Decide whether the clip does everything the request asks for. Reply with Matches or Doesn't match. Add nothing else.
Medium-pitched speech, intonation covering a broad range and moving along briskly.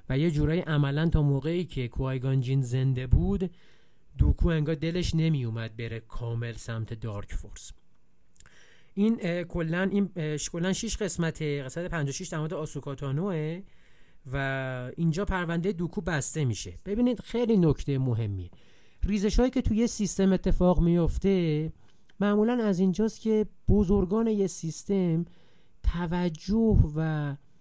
Doesn't match